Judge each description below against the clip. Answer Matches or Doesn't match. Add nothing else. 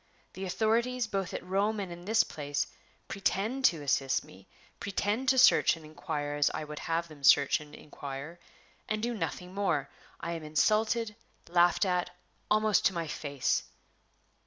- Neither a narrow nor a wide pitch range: Doesn't match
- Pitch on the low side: Doesn't match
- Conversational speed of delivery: Matches